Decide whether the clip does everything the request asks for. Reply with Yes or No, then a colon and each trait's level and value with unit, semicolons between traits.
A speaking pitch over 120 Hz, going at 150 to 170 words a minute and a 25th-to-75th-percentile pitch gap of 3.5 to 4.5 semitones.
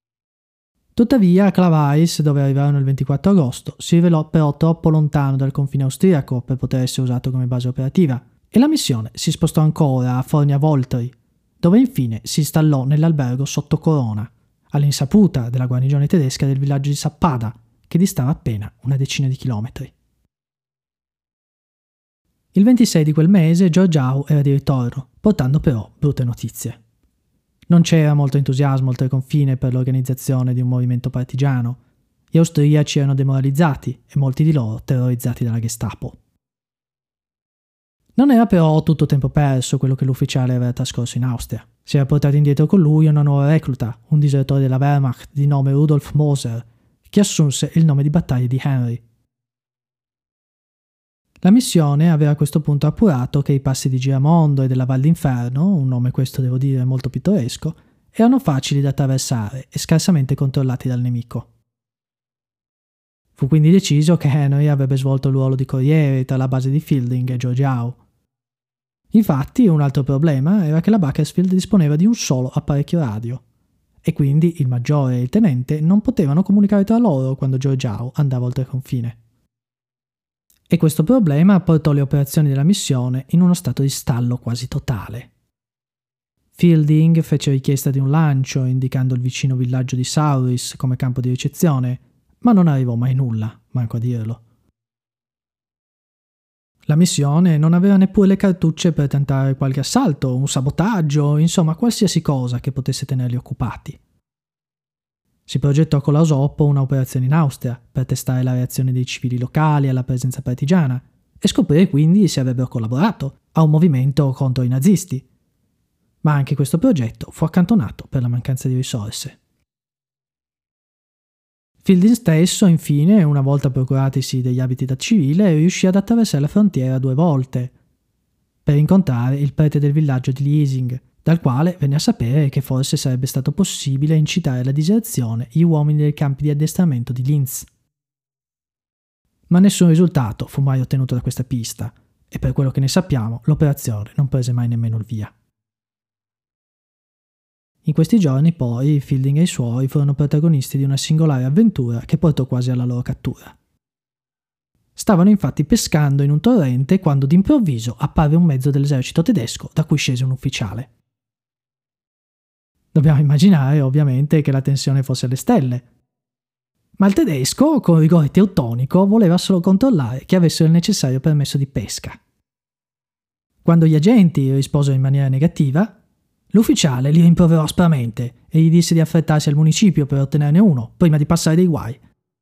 Yes: medium, 140 Hz; average, 155 wpm; average, 3.8 semitones